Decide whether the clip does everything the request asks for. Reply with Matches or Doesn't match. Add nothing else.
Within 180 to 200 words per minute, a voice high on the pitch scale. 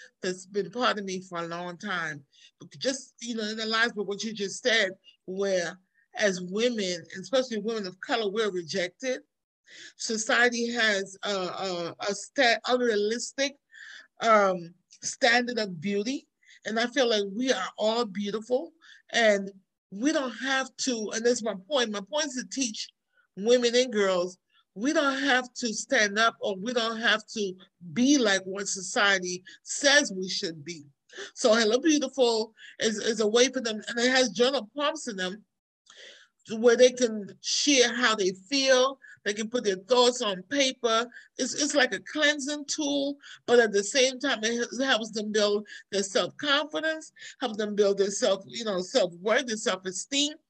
Doesn't match